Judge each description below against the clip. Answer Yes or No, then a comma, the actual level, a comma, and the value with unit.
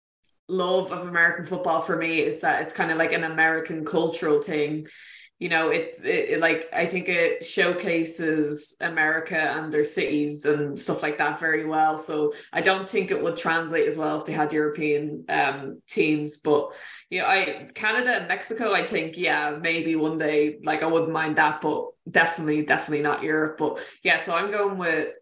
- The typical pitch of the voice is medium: Yes, medium, 160 Hz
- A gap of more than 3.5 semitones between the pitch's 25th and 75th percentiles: No, average, 2.7 semitones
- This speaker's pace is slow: No, average, 195 wpm